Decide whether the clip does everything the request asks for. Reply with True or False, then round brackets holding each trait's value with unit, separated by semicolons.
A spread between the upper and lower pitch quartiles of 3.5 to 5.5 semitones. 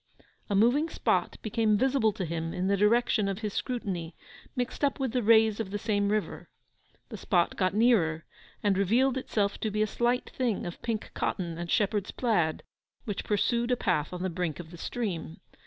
True (4.3 semitones)